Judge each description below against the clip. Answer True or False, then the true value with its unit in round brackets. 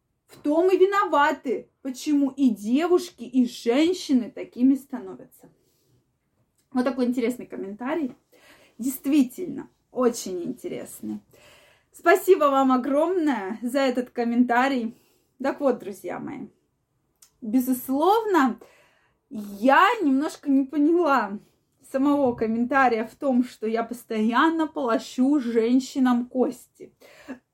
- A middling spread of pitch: True (3.4 semitones)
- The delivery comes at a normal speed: False (95 wpm)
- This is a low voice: False (265 Hz)